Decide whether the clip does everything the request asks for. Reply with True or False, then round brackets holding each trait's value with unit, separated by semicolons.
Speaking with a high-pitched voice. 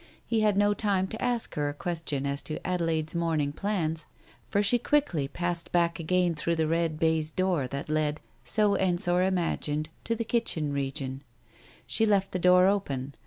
False (170 Hz)